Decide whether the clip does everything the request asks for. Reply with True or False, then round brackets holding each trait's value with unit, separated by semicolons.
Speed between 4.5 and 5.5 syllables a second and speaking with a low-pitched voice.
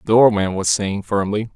True (5.2 syllables/s; 105 Hz)